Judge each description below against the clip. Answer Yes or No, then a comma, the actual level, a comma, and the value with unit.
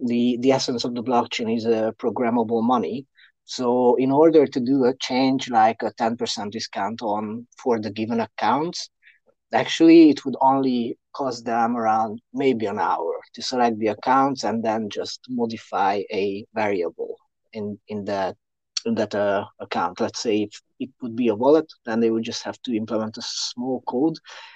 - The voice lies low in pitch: Yes, low, 120 Hz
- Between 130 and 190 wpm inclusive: Yes, average, 180 wpm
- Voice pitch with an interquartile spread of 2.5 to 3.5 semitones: Yes, average, 3.2 semitones